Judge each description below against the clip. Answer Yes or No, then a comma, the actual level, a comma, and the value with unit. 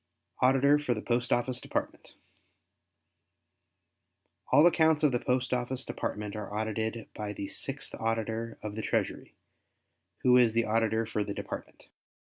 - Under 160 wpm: Yes, average, 140 wpm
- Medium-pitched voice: No, low, 115 Hz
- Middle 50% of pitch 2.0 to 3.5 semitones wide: Yes, narrow, 2.5 semitones